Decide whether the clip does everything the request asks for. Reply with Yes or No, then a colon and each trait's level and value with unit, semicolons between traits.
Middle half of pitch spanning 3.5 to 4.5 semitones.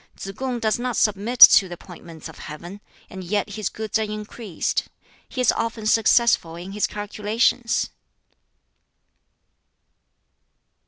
No: average, 3.1 semitones